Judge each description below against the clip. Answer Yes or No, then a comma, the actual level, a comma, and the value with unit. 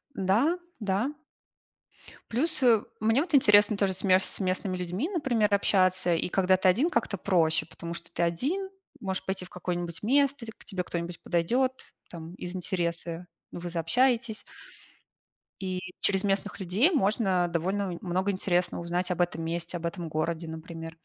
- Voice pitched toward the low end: No, medium, 185 Hz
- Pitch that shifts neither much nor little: Yes, average, 4.0 semitones